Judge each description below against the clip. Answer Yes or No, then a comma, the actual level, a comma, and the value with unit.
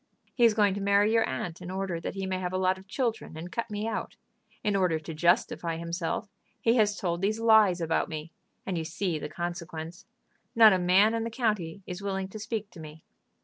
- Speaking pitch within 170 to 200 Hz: Yes, high, 190 Hz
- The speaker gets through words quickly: Yes, fast, 225 wpm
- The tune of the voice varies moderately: Yes, average, 3.8 semitones